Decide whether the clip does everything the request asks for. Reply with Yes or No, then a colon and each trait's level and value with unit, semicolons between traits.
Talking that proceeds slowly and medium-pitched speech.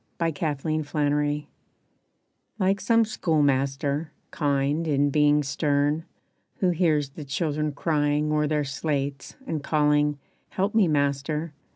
Yes: slow, 115 wpm; medium, 150 Hz